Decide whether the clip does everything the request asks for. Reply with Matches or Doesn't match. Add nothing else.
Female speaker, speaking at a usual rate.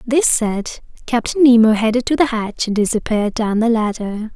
Matches